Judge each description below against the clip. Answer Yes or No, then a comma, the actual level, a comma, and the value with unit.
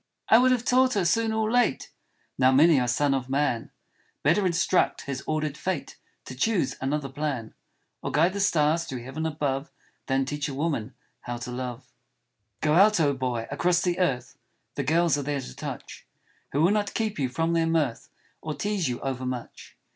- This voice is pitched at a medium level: Yes, medium, 150 Hz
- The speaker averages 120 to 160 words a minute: No, average, 200 wpm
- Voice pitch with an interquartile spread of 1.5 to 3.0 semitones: No, average, 4.9 semitones